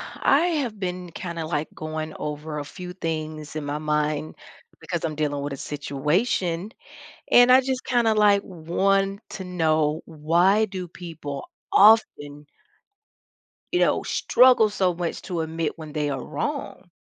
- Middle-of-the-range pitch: Yes, medium, 165 Hz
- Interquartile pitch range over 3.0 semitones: Yes, average, 4.5 semitones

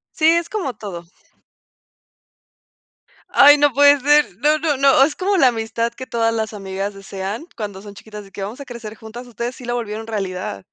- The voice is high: Yes, high, 230 Hz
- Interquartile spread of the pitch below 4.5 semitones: No, wide, 5.5 semitones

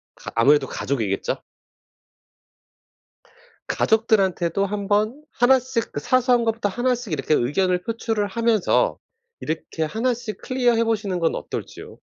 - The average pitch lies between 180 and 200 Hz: No, high, 215 Hz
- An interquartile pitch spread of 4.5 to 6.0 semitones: Yes, average, 5.1 semitones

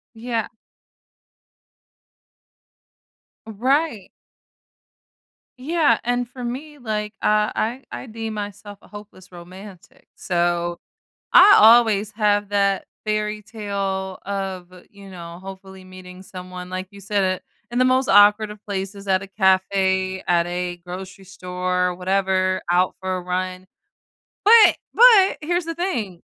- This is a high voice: Yes, high, 200 Hz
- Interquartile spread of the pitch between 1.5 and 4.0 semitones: Yes, average, 2.9 semitones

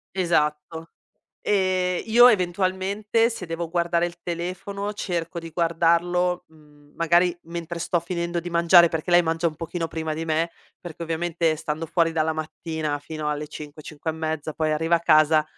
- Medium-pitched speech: Yes, medium, 170 Hz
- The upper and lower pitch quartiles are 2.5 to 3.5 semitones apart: No, narrow, 1.8 semitones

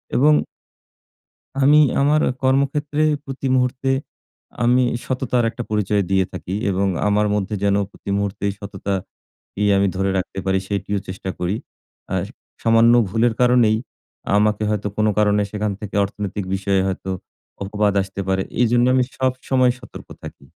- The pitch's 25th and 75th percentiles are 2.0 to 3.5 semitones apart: No, average, 4.1 semitones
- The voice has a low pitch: Yes, low, 105 Hz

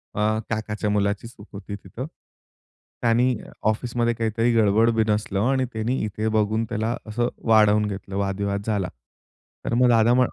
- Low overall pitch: Yes, low, 110 Hz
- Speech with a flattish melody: Yes, narrow, 2.1 semitones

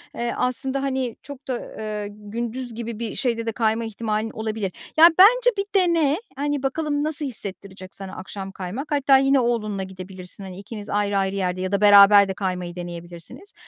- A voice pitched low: No, high, 220 Hz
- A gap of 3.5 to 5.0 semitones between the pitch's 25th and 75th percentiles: No, wide, 5.5 semitones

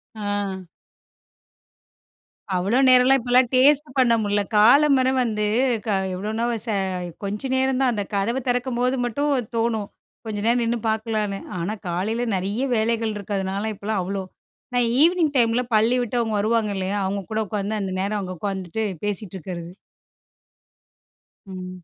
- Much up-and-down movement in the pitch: No, average, 3.6 semitones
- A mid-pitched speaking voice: No, high, 220 Hz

